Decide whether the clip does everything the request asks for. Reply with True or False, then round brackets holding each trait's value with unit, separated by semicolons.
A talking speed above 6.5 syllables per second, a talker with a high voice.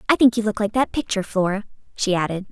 True (7.1 syllables/s; 210 Hz)